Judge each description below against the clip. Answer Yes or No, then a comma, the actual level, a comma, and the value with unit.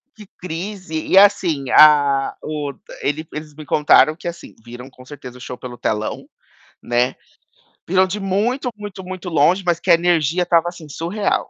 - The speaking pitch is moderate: Yes, medium, 160 Hz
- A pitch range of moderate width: Yes, average, 4.6 semitones